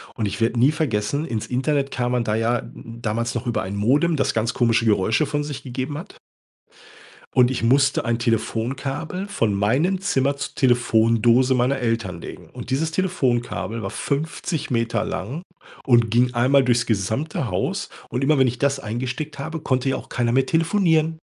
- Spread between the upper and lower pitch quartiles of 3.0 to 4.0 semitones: Yes, average, 3.6 semitones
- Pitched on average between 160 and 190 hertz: No, low, 125 Hz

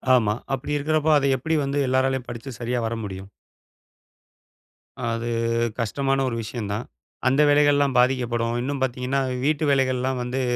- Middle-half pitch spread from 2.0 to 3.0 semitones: Yes, average, 2.7 semitones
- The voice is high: No, low, 130 Hz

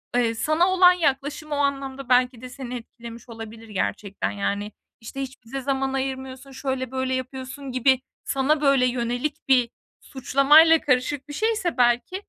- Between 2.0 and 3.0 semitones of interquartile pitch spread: Yes, narrow, 2.4 semitones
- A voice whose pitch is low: No, very high, 265 Hz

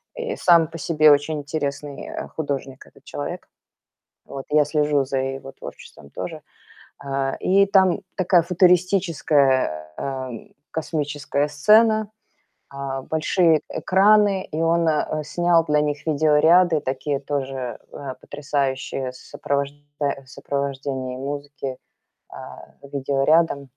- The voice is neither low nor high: Yes, medium, 145 Hz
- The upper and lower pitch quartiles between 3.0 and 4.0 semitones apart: Yes, average, 3.4 semitones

